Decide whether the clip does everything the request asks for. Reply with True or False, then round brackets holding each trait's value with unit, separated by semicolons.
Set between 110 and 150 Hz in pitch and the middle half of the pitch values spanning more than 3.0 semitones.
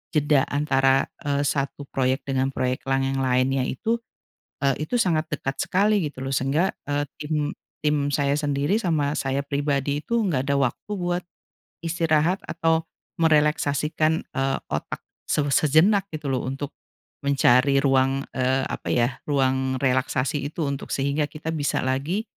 False (140 Hz; 2.6 semitones)